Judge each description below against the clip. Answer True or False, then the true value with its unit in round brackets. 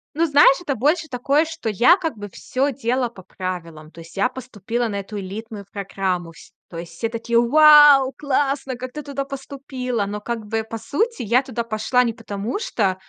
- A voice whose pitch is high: True (235 Hz)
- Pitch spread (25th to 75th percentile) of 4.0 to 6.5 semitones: True (5.2 semitones)